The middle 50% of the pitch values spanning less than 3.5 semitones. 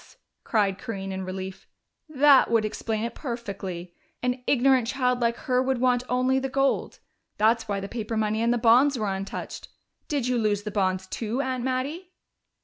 No: average, 3.8 semitones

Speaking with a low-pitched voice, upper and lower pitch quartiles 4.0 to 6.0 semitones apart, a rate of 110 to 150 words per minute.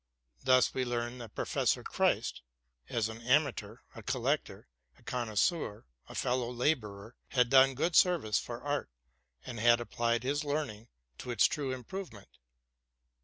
No: low, 125 Hz; average, 3.2 semitones; average, 140 wpm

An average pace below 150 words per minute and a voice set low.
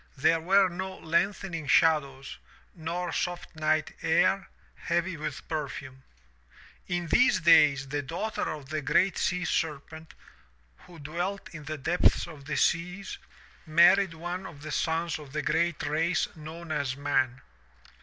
No: average, 140 wpm; medium, 160 Hz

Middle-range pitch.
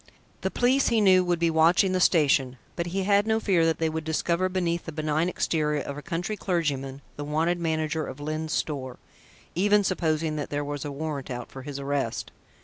Yes: medium, 160 Hz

